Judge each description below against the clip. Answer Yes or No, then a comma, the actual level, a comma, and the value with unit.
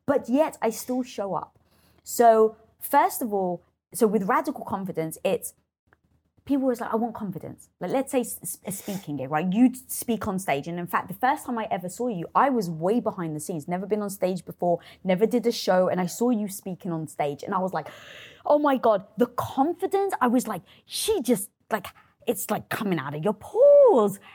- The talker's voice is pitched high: Yes, high, 215 Hz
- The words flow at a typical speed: No, fast, 210 wpm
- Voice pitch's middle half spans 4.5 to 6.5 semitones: Yes, average, 5.3 semitones